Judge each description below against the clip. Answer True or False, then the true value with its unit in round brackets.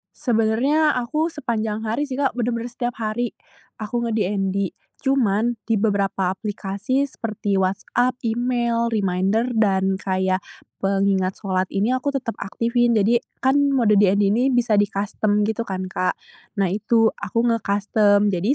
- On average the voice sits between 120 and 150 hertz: False (215 Hz)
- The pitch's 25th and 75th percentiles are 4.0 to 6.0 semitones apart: False (3.4 semitones)